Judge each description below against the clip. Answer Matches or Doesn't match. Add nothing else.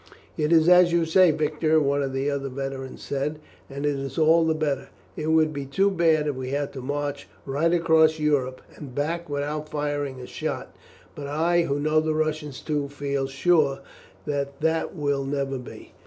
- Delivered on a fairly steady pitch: Matches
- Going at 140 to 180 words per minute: Doesn't match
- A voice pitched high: Doesn't match